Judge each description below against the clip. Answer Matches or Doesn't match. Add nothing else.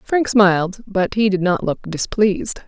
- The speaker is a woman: Matches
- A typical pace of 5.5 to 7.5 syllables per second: Doesn't match